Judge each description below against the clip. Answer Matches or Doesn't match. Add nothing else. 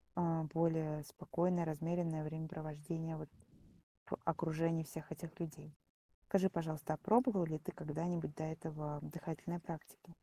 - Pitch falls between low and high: Matches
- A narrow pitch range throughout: Matches